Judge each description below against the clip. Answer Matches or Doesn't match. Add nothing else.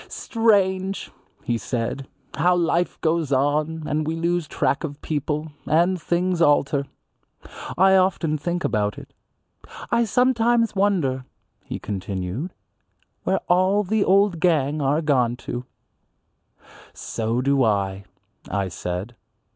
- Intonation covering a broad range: Matches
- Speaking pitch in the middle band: Matches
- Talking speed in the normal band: Doesn't match